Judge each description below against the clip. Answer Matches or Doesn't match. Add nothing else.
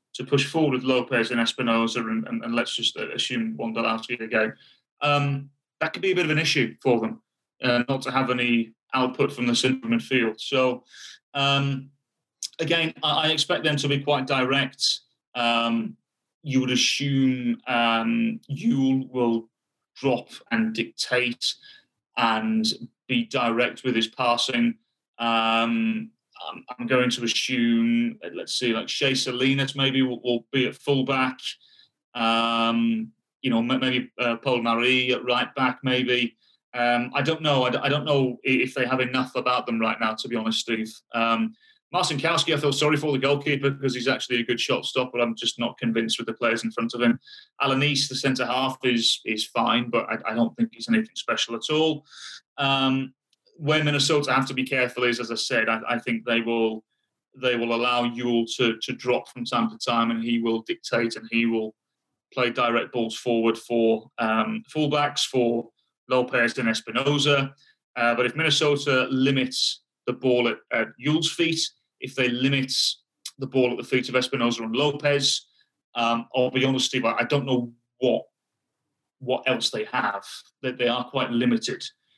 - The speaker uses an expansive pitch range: Doesn't match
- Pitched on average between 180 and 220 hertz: Doesn't match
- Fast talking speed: Doesn't match